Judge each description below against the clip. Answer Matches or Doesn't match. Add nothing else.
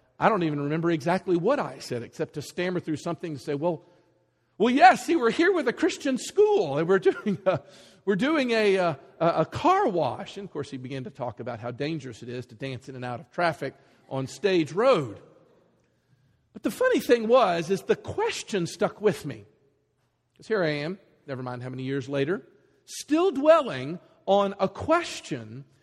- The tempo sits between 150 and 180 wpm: Doesn't match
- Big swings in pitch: Matches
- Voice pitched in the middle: Matches